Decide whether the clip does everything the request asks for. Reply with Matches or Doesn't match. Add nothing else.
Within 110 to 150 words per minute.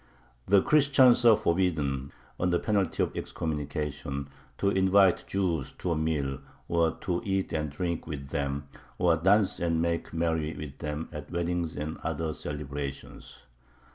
Matches